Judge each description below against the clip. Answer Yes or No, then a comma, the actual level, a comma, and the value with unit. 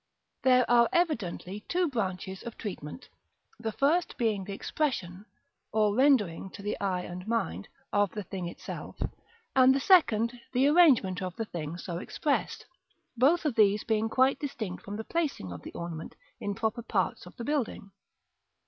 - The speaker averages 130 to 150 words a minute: No, average, 165 wpm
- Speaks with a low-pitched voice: No, high, 215 Hz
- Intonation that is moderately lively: No, wide, 5.7 semitones